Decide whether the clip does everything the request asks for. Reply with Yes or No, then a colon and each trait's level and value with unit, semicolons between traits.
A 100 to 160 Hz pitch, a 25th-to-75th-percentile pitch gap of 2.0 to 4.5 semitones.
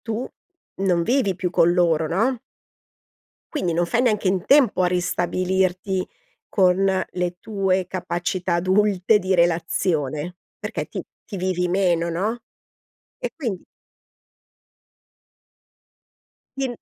No: medium, 185 Hz; narrow, 2.3 semitones